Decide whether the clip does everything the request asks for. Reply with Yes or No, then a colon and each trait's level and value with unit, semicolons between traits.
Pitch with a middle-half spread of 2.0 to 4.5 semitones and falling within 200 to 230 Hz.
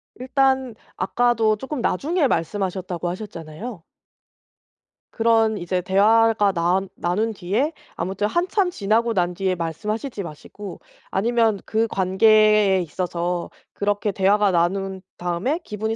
Yes: average, 3.8 semitones; high, 205 Hz